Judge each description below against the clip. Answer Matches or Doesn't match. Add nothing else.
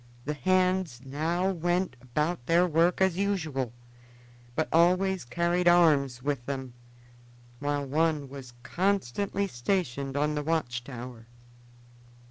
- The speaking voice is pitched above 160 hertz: Doesn't match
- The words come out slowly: Matches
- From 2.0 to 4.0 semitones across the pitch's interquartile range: Doesn't match